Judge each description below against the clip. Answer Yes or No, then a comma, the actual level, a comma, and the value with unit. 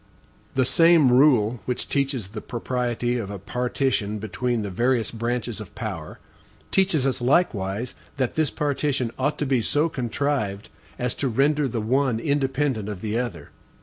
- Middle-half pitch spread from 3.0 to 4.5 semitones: Yes, average, 3.8 semitones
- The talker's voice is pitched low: Yes, low, 125 Hz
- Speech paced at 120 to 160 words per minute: Yes, average, 155 wpm